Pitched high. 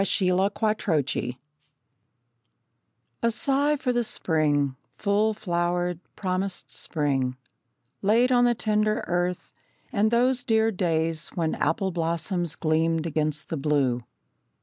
No: medium, 175 Hz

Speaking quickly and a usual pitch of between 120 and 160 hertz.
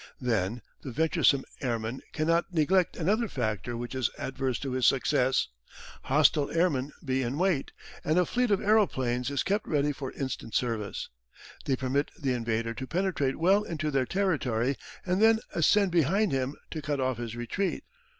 No: average, 165 wpm; medium, 140 Hz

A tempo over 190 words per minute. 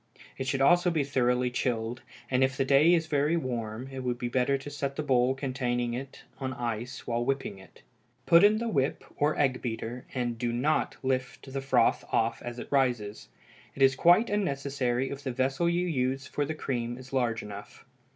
Yes: average, 200 wpm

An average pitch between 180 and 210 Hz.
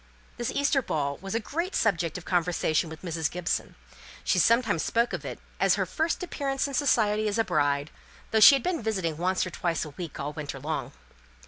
Yes: medium, 185 Hz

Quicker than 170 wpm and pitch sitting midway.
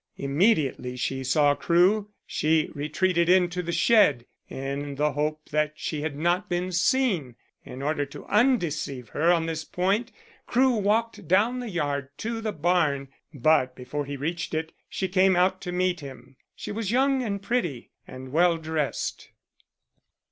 No: average, 155 wpm; medium, 165 Hz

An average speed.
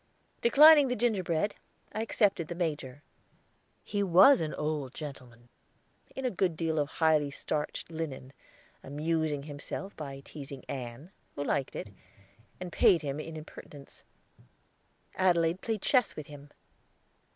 No: slow, 130 wpm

